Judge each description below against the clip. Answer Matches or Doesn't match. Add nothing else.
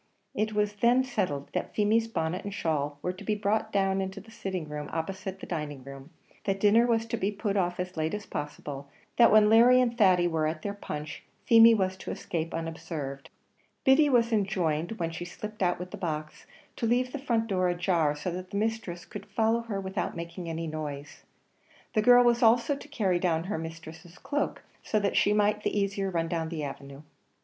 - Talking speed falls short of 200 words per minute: Doesn't match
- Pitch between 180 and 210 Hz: Matches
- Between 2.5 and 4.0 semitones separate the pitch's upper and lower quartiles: Doesn't match